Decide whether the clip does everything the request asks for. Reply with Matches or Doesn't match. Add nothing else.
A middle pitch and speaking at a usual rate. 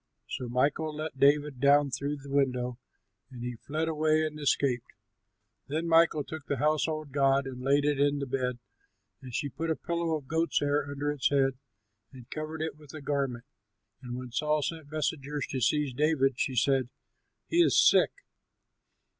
Matches